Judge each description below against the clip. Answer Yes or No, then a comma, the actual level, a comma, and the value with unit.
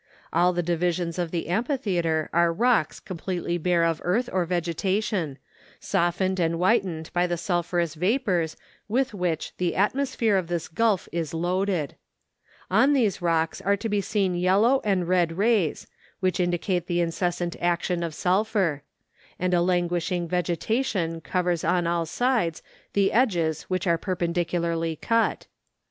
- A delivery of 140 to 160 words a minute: Yes, average, 145 wpm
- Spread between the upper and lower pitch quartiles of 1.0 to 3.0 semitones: Yes, average, 2.7 semitones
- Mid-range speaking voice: Yes, medium, 180 Hz